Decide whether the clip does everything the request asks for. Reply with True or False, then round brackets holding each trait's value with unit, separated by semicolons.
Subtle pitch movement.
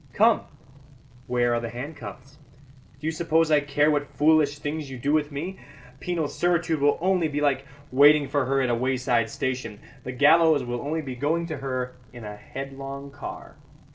False (3.2 semitones)